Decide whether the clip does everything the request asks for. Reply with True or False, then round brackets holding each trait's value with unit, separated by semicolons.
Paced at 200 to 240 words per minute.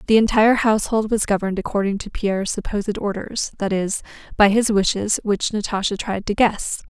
False (175 wpm)